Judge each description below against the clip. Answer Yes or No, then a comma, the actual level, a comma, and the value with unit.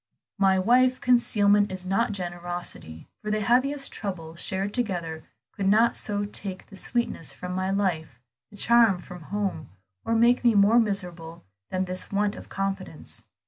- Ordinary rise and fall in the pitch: Yes, average, 3.5 semitones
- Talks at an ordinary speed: Yes, average, 155 wpm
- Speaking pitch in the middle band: No, high, 195 Hz